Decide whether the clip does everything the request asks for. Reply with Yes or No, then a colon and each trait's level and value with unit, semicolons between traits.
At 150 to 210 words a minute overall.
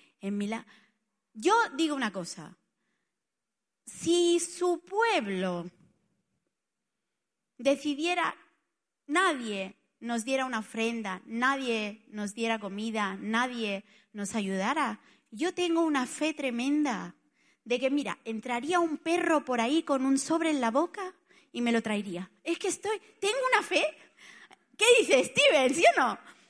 No: average, 130 wpm